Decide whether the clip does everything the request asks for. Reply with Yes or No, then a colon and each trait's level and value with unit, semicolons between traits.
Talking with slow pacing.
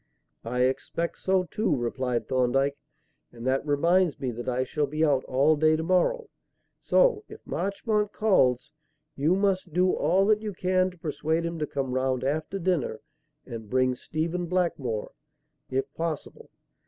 No: average, 155 wpm